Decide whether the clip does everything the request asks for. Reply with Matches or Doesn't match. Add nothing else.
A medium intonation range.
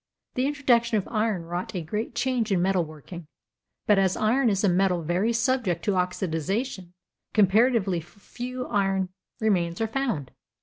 Matches